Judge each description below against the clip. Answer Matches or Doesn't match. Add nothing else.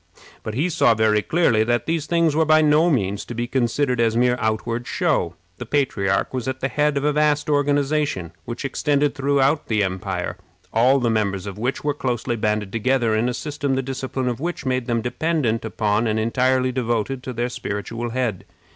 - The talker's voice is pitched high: Doesn't match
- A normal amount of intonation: Matches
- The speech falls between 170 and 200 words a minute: Matches